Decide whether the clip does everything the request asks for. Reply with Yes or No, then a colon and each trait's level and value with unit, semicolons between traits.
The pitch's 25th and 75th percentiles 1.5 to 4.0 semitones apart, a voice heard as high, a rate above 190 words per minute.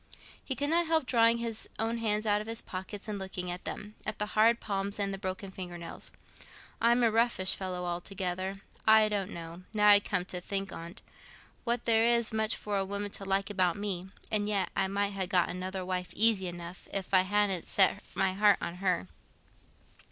Yes: narrow, 2.6 semitones; high, 200 Hz; average, 200 wpm